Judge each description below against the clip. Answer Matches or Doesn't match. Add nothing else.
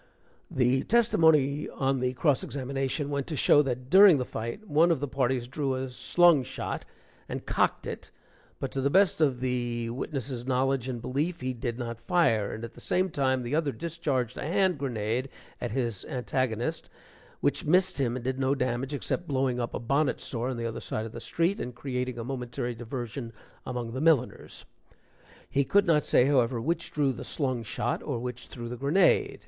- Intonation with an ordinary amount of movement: Matches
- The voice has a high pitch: Doesn't match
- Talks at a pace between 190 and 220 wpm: Matches